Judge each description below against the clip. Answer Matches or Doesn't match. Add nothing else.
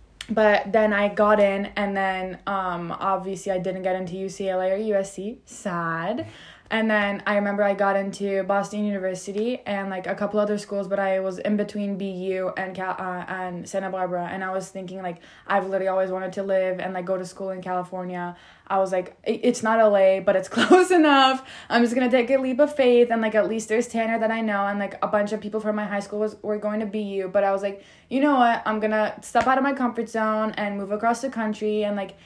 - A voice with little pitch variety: Matches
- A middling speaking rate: Doesn't match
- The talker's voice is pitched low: Doesn't match